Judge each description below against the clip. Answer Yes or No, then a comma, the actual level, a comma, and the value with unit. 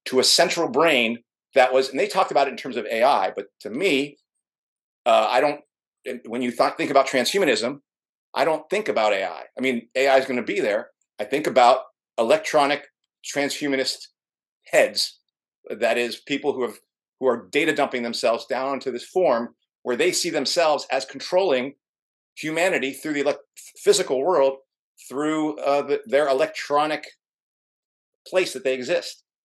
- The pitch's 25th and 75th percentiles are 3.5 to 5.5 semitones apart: No, average, 3.1 semitones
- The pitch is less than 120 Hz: No, medium, 140 Hz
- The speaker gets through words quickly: No, average, 165 wpm